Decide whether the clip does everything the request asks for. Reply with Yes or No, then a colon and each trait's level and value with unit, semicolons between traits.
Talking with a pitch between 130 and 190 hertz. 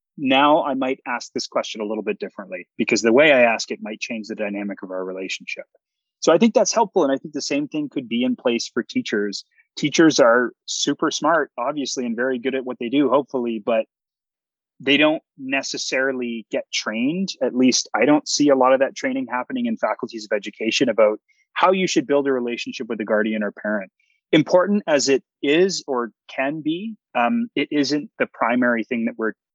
Yes: low, 135 Hz